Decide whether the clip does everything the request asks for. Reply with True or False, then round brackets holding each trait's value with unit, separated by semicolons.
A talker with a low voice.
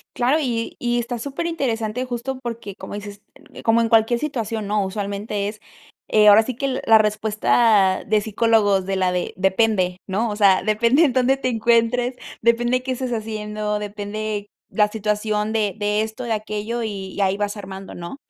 False (215 Hz)